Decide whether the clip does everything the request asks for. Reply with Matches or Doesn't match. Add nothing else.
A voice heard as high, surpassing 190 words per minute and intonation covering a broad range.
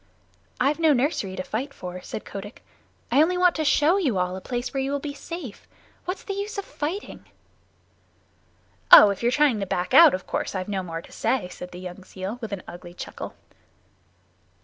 Matches